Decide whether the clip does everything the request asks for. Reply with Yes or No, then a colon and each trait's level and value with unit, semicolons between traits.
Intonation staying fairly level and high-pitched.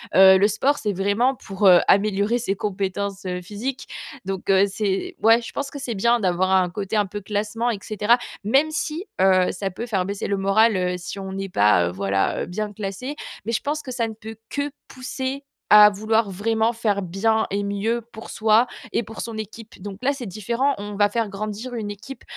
No: average, 3.1 semitones; high, 210 Hz